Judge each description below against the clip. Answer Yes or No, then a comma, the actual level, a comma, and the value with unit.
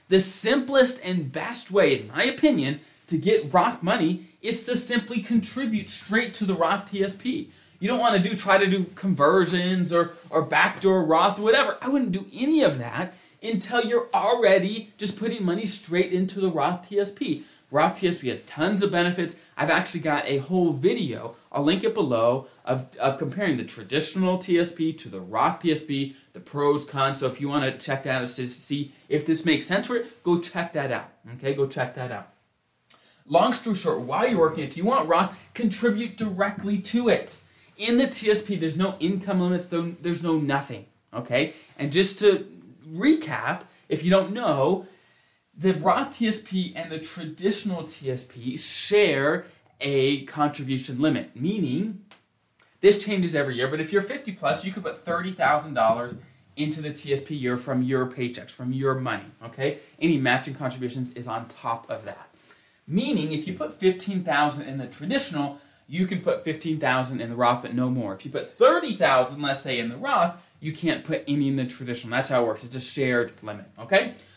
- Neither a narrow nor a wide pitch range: No, wide, 6.3 semitones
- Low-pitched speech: No, medium, 170 Hz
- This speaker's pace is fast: No, average, 185 wpm